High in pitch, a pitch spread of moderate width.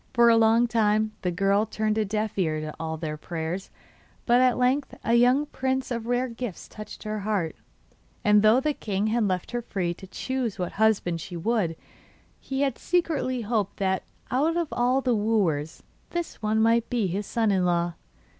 Yes: high, 220 Hz; average, 4.4 semitones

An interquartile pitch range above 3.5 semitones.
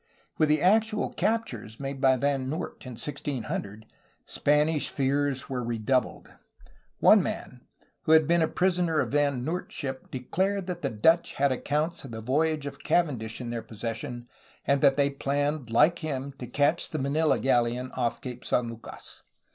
Yes: average, 4.0 semitones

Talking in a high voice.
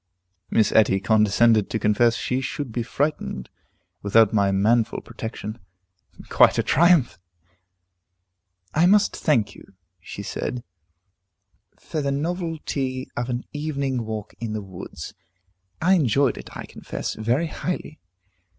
No: low, 120 Hz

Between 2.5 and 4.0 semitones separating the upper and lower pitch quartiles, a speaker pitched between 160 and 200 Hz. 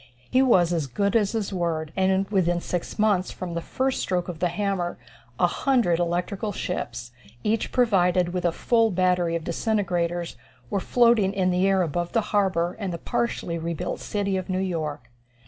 Yes: average, 2.8 semitones; medium, 185 Hz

